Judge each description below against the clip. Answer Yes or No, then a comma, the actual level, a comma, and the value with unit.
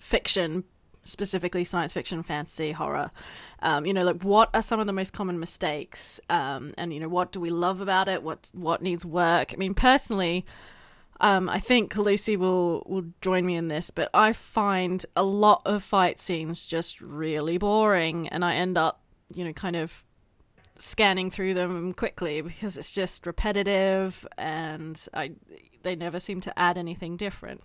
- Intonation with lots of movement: No, narrow, 2.4 semitones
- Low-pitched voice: No, medium, 180 Hz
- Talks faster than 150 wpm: Yes, average, 175 wpm